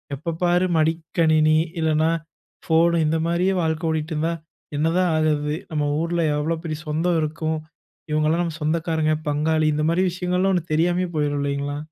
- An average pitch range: No, narrow, 1.8 semitones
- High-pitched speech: No, medium, 160 Hz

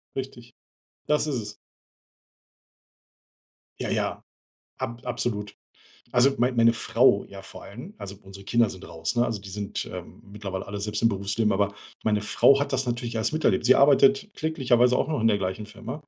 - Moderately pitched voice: No, low, 115 Hz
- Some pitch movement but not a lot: Yes, average, 3.7 semitones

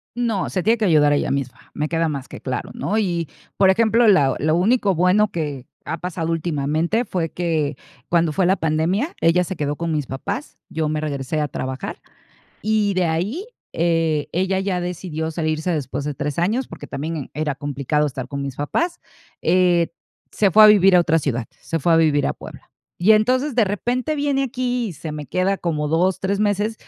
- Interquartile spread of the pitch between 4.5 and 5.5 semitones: Yes, average, 5.0 semitones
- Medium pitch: Yes, medium, 170 Hz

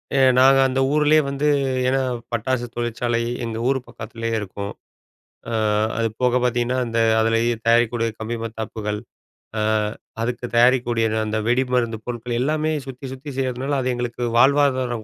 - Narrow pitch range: Yes, narrow, 2.2 semitones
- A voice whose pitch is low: Yes, low, 120 Hz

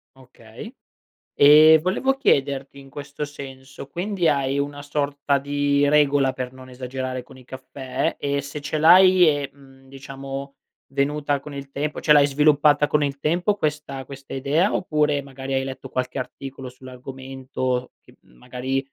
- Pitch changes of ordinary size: No, narrow, 1.8 semitones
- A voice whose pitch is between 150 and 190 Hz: No, medium, 140 Hz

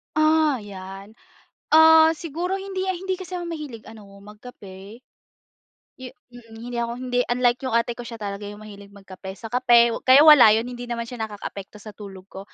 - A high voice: Yes, high, 235 Hz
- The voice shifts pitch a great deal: Yes, wide, 6.5 semitones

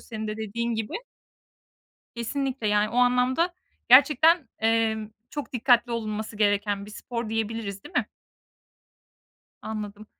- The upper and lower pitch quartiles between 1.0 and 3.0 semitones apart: Yes, average, 2.7 semitones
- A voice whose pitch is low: No, high, 225 Hz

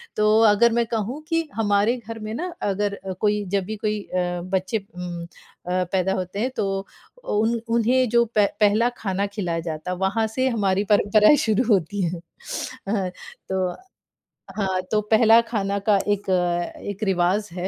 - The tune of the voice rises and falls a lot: No, average, 2.8 semitones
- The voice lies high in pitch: Yes, high, 205 Hz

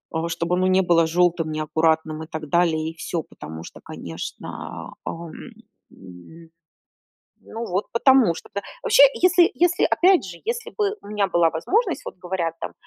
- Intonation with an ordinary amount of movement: No, wide, 6.0 semitones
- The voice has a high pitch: No, medium, 175 Hz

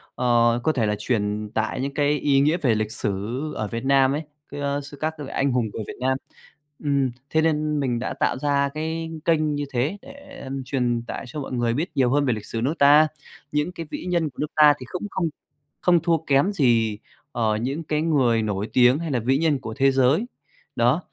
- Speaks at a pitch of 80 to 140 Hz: Yes, low, 135 Hz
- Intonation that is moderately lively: Yes, average, 4.2 semitones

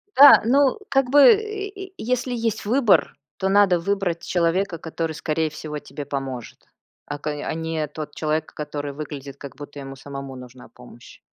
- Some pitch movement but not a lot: No, wide, 7.5 semitones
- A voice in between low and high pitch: Yes, medium, 160 Hz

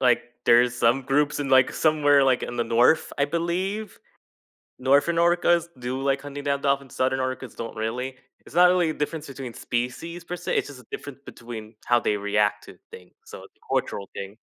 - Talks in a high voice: No, low, 135 Hz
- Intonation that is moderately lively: Yes, average, 4.2 semitones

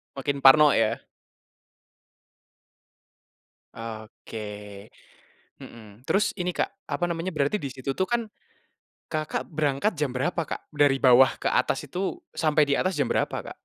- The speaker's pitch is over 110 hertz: Yes, medium, 140 Hz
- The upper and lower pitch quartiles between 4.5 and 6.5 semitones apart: Yes, average, 5.3 semitones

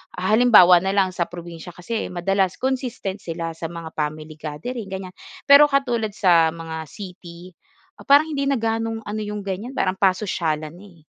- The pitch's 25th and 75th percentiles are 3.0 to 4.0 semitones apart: No, average, 4.9 semitones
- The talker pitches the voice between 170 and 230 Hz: Yes, high, 190 Hz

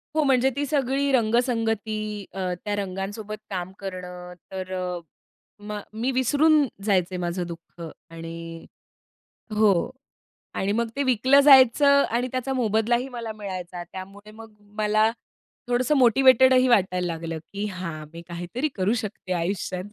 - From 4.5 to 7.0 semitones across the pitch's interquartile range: Yes, wide, 5.6 semitones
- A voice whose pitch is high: Yes, high, 210 Hz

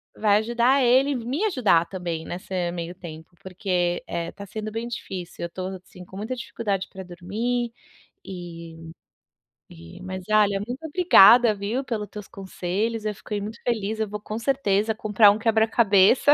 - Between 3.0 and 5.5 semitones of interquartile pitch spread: Yes, average, 3.9 semitones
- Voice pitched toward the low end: No, high, 210 Hz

